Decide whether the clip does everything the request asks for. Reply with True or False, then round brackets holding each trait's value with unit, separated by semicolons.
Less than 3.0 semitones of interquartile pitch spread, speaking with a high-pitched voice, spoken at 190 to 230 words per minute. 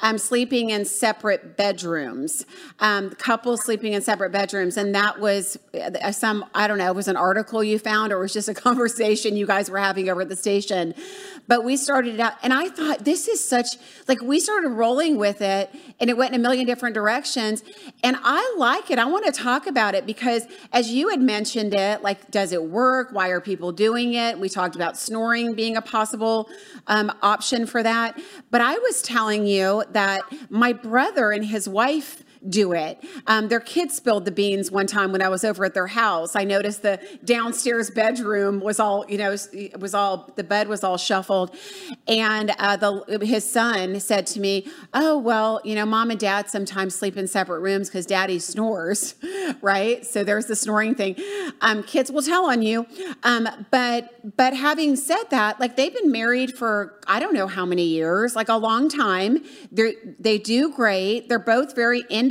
False (3.7 semitones; 220 Hz; 200 wpm)